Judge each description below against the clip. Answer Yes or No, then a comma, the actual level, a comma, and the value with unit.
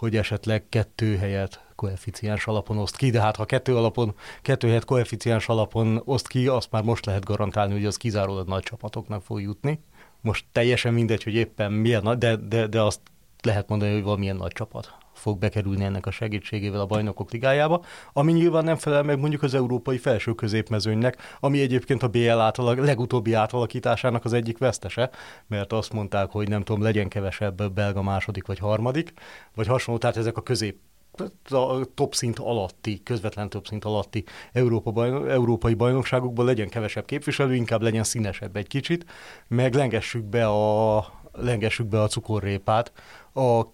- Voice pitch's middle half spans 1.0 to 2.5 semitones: No, average, 2.9 semitones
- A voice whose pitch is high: No, low, 115 Hz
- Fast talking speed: Yes, fast, 170 wpm